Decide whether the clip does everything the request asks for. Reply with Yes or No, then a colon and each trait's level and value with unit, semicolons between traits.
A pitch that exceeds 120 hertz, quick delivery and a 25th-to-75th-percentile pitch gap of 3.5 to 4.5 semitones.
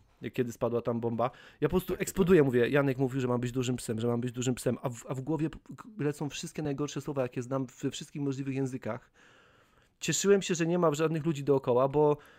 Yes: medium, 140 Hz; fast, 220 wpm; average, 4.0 semitones